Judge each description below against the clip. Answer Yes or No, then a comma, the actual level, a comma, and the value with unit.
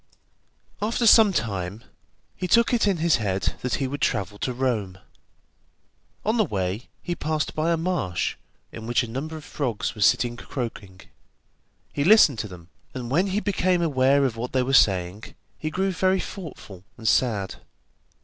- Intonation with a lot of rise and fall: Yes, wide, 8.2 semitones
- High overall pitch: No, low, 130 Hz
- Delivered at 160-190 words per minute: Yes, average, 170 wpm